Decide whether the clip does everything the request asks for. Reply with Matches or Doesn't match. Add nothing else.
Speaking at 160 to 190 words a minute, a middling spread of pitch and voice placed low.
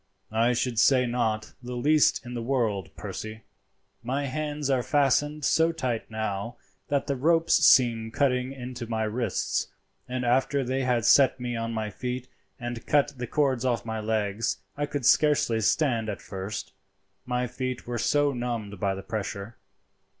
Matches